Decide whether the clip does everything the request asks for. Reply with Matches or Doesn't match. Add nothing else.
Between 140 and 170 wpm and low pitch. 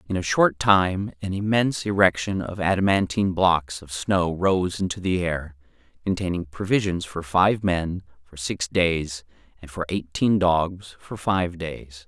Matches